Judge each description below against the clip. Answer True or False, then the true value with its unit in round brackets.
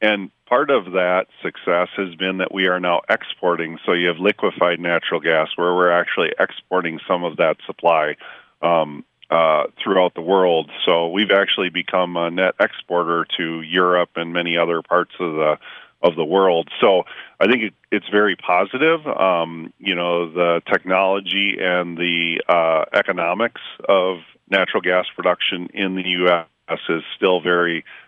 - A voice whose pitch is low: True (90 Hz)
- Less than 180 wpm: True (160 wpm)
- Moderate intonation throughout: False (1.7 semitones)